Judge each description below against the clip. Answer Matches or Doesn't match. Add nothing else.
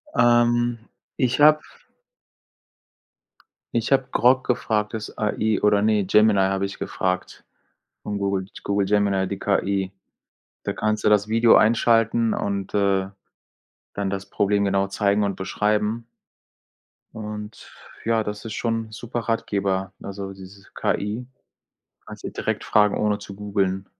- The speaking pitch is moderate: Doesn't match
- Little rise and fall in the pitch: Matches